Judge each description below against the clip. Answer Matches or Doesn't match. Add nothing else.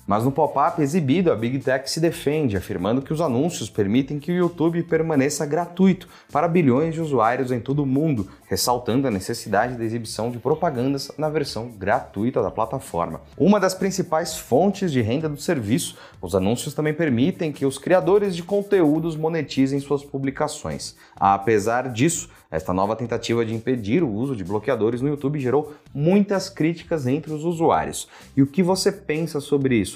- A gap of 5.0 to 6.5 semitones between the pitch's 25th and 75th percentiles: Matches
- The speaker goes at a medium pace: Matches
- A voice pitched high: Doesn't match